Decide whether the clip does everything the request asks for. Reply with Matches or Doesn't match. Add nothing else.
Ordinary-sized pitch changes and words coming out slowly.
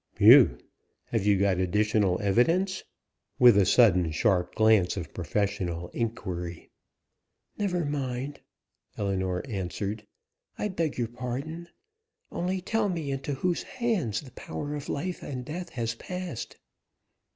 Doesn't match